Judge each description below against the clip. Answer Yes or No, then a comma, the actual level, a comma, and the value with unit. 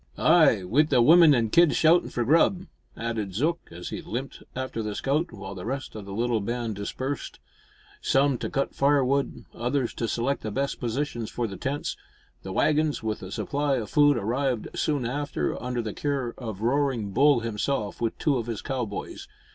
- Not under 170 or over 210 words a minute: Yes, average, 185 wpm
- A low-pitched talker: Yes, low, 125 Hz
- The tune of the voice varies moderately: Yes, average, 4.2 semitones